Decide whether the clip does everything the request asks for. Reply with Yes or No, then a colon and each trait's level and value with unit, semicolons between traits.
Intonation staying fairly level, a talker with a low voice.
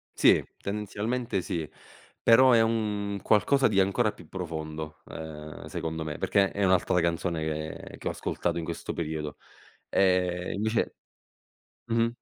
No: average, 4.8 semitones; very low, 95 Hz